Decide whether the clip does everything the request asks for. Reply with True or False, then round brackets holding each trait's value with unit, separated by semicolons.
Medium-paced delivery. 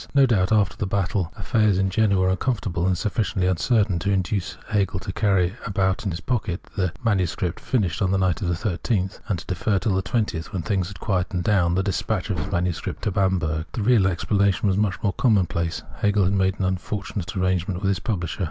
False (210 wpm)